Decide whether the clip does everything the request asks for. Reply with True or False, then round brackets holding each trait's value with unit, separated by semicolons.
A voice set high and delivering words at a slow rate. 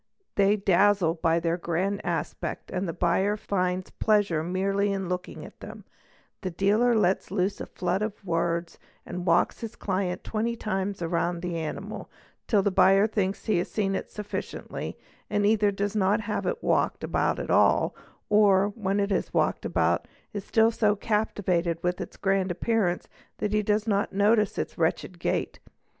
False (195 Hz; 175 wpm)